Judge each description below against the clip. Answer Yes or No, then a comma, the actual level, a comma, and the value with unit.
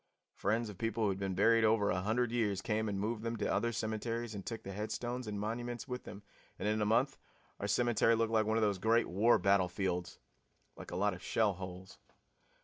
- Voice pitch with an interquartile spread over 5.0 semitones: No, narrow, 2.6 semitones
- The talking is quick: Yes, fast, 220 wpm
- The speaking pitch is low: Yes, low, 110 Hz